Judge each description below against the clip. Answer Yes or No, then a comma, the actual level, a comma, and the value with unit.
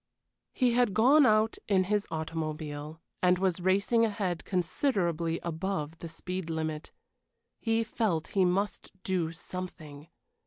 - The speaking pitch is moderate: Yes, medium, 180 Hz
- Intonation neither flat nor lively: Yes, average, 4.3 semitones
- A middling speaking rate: No, slow, 125 wpm